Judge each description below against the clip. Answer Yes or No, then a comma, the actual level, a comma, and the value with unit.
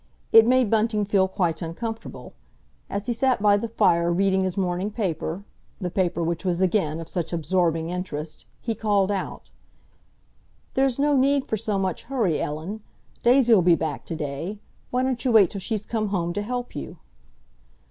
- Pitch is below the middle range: No, high, 195 Hz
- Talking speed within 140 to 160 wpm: No, average, 170 wpm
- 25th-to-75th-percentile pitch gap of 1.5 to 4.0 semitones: No, average, 4.7 semitones